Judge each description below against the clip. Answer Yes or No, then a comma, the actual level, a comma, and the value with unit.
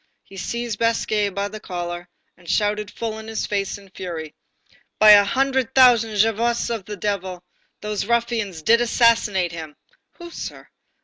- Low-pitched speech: No, high, 210 Hz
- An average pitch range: Yes, average, 3.6 semitones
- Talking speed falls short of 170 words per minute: Yes, average, 150 wpm